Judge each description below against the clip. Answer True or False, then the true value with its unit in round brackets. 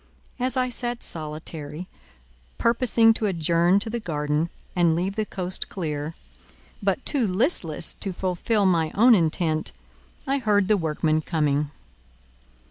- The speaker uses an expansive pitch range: True (5.9 semitones)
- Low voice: False (180 Hz)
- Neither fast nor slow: False (130 wpm)